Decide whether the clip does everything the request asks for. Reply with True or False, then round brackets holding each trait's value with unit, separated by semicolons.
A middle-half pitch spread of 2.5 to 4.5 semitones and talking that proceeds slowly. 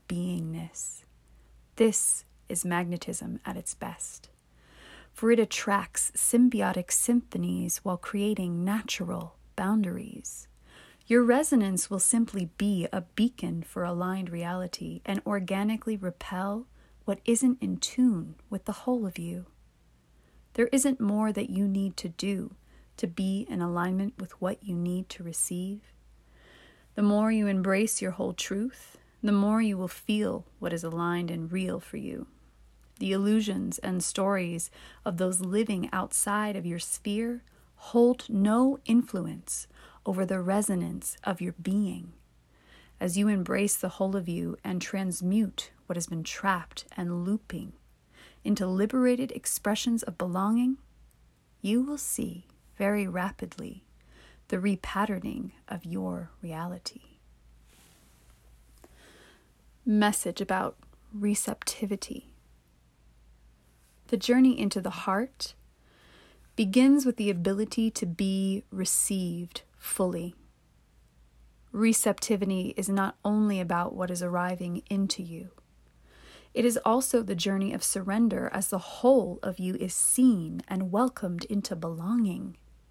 True (3.6 semitones; 120 wpm)